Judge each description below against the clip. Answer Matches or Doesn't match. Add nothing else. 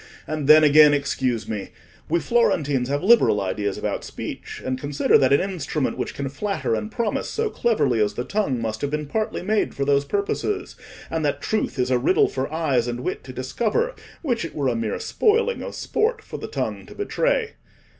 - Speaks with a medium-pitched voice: Matches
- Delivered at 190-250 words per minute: Matches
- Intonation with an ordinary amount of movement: Doesn't match